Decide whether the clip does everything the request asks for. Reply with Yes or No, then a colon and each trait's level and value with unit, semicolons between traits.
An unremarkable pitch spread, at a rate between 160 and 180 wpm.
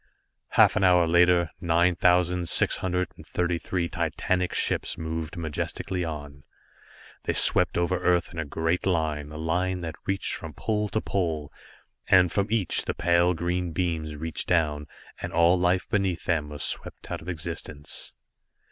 No: narrow, 2.0 semitones; average, 165 wpm